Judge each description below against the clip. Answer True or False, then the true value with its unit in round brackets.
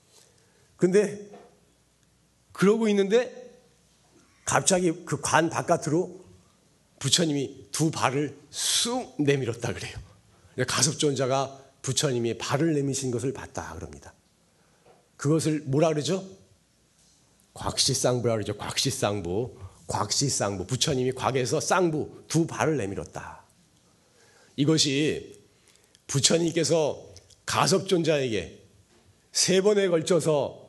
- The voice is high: False (140 Hz)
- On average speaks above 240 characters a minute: False (225 characters per minute)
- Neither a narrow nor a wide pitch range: False (6.0 semitones)